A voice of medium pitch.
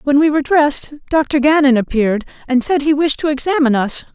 No: very high, 280 Hz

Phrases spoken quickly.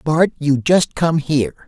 No: average, 180 wpm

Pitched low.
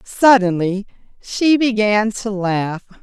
No: high, 210 Hz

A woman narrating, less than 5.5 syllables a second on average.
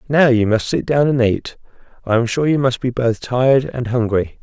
No: male; 5.0 syllables/s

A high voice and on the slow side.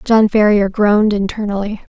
Yes: high, 205 Hz; slow, 125 wpm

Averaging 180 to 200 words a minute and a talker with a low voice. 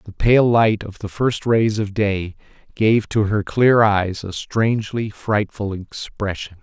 No: average, 165 wpm; low, 105 Hz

